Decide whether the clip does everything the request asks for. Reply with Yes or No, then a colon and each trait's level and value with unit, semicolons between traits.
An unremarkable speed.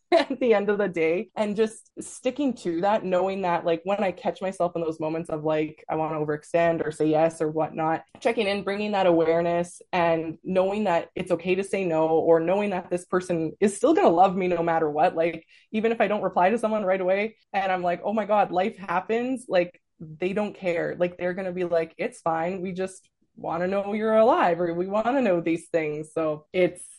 No: fast, 235 wpm